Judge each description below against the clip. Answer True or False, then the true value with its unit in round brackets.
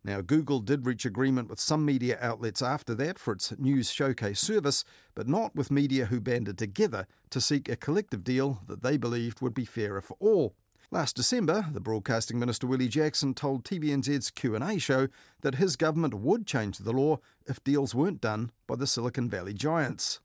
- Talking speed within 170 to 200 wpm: True (185 wpm)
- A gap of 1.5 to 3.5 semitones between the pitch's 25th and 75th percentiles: False (3.9 semitones)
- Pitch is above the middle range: False (130 Hz)